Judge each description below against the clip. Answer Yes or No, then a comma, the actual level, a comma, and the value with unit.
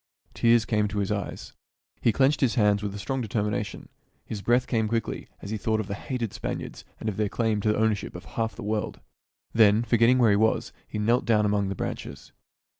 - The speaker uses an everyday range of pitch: No, narrow, 2.0 semitones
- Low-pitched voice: Yes, low, 110 Hz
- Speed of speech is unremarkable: No, fast, 210 wpm